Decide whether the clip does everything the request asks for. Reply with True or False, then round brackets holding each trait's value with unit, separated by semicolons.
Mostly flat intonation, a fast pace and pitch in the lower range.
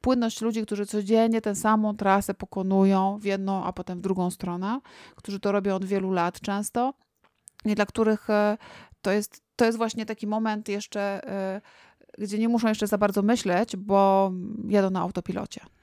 False (2.2 semitones; 165 wpm; 205 Hz)